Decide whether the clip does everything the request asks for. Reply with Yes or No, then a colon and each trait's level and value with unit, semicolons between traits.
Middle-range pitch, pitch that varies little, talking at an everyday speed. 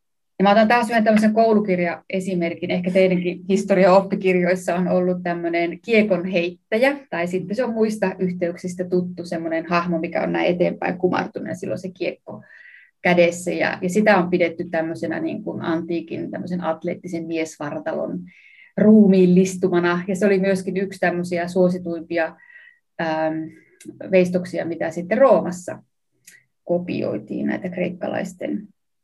Yes: medium, 180 Hz; narrow, 2.1 semitones; average, 120 wpm